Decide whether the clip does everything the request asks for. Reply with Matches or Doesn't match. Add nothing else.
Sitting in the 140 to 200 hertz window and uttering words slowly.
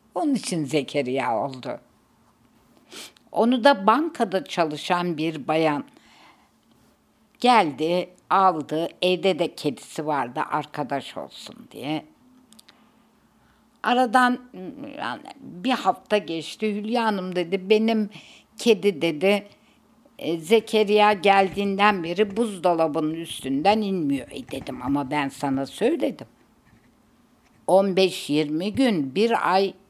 Matches